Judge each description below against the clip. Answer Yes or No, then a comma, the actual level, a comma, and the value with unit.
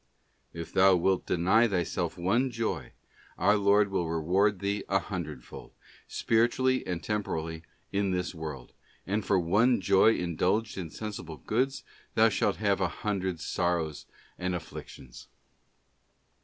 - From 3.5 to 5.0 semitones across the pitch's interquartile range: Yes, average, 3.8 semitones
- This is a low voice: Yes, very low, 95 Hz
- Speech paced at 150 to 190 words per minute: No, slow, 135 wpm